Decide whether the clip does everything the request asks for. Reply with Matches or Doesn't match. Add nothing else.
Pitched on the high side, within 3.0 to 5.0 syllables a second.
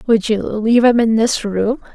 Matches